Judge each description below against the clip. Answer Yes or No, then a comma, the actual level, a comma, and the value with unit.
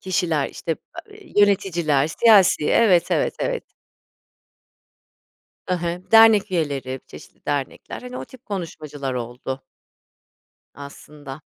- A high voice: No, medium, 170 Hz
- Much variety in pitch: Yes, wide, 6.3 semitones